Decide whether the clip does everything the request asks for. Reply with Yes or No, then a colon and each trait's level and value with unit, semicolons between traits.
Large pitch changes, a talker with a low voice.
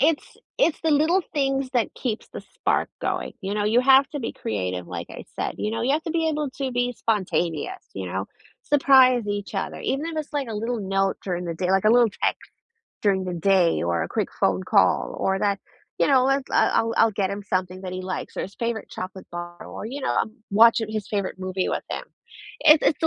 No: wide, 6.3 semitones; high, 215 Hz